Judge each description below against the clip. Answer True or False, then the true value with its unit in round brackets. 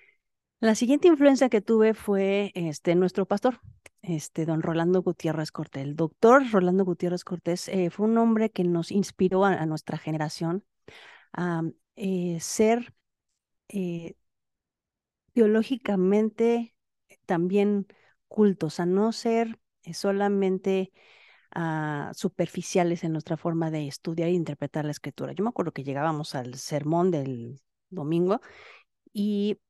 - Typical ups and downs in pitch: True (4.1 semitones)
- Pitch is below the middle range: False (180 Hz)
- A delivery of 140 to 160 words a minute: False (130 wpm)